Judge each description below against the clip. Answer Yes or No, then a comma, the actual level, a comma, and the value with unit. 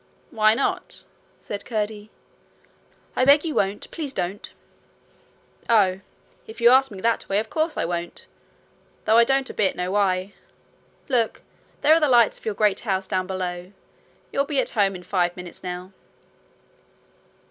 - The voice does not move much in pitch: No, average, 4.7 semitones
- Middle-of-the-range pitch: No, high, 205 Hz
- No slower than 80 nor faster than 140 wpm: No, average, 160 wpm